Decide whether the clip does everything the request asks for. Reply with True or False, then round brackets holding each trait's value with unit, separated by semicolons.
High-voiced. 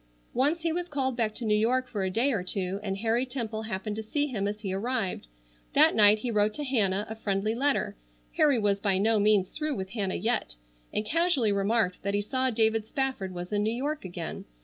True (215 Hz)